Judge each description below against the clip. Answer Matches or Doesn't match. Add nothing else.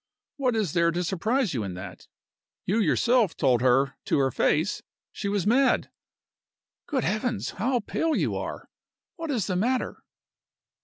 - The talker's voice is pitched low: Doesn't match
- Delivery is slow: Doesn't match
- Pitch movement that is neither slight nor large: Doesn't match